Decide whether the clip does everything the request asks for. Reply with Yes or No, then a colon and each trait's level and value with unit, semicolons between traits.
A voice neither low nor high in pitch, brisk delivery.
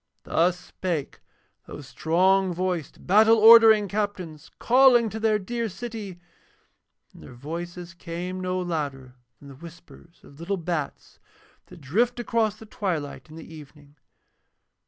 No: medium, 180 Hz; slow, 135 wpm